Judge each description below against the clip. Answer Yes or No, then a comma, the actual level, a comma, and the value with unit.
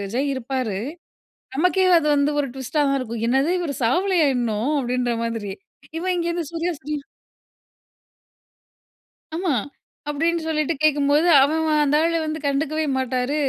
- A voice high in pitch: Yes, very high, 290 Hz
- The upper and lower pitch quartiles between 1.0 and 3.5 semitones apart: No, average, 3.9 semitones